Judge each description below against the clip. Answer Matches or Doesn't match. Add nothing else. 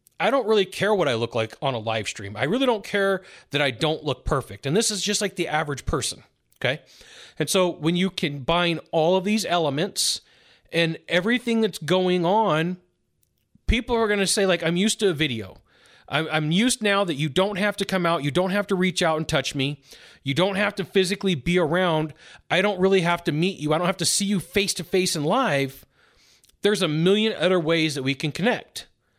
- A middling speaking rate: Doesn't match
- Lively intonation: Doesn't match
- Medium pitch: Matches